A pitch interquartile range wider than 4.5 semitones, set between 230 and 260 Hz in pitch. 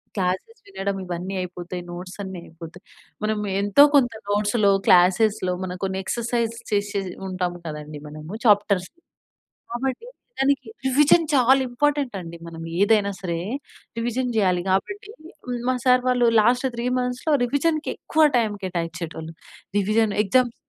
No: wide, 5.4 semitones; high, 205 Hz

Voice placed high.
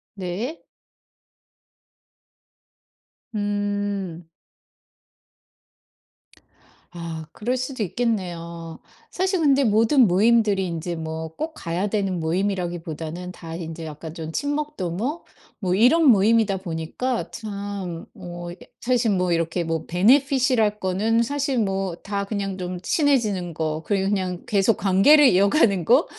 Yes: high, 195 Hz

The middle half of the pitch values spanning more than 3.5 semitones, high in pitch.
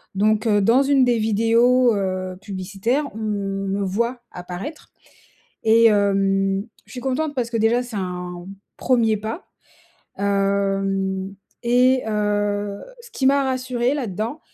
Yes: average, 4.0 semitones; high, 215 Hz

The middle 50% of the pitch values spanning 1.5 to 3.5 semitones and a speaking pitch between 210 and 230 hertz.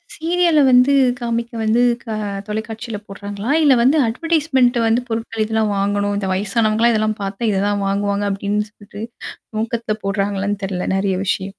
Yes: average, 2.7 semitones; high, 215 Hz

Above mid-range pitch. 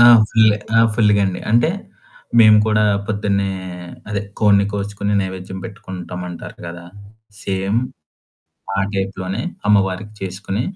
No: low, 100 Hz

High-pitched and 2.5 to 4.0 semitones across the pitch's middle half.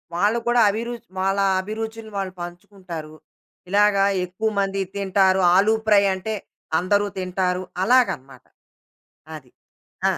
Yes: high, 195 Hz; average, 2.9 semitones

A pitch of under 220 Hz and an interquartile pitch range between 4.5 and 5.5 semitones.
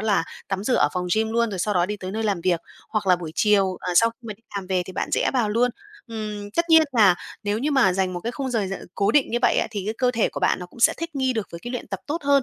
No: high, 210 Hz; average, 4.0 semitones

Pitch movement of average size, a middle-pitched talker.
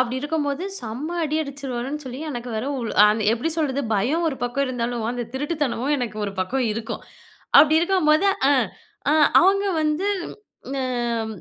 No: average, 4.1 semitones; very high, 265 Hz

